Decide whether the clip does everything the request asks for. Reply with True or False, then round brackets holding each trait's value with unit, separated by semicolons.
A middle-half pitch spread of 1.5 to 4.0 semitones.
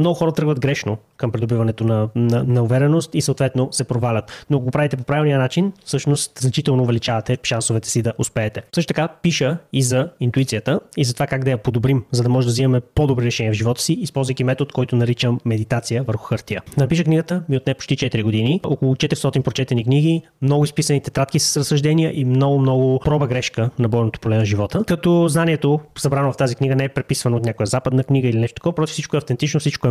True (3.4 semitones)